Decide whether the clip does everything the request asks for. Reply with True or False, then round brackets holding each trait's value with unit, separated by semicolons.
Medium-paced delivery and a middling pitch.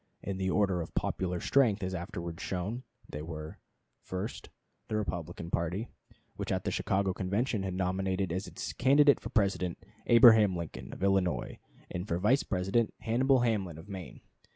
False (160 wpm; 95 Hz)